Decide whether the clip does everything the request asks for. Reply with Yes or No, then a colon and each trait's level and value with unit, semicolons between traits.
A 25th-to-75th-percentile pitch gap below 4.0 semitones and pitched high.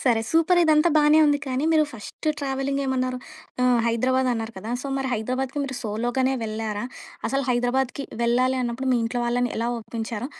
Yes: narrow, 2.4 semitones; very high, 255 Hz